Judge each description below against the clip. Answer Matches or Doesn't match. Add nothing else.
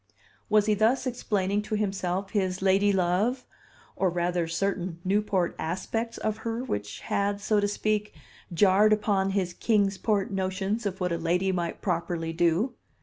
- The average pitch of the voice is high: Matches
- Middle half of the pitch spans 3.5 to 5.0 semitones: Doesn't match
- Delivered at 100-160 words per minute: Matches